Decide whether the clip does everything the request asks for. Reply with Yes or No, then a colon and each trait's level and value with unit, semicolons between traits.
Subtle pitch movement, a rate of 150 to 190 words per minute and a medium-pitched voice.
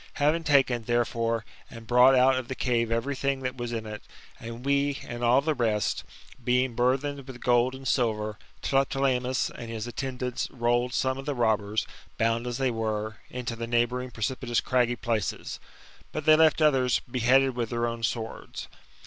No: narrow, 2.3 semitones; average, 175 wpm; low, 125 Hz